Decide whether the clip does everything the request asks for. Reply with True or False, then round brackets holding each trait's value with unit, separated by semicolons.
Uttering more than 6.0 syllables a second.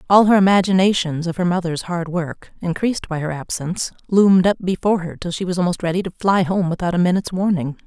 True (6.3 syllables/s)